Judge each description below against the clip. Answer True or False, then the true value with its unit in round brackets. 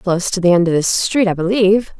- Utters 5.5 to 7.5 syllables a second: True (6.2 syllables/s)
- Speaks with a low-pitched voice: False (190 Hz)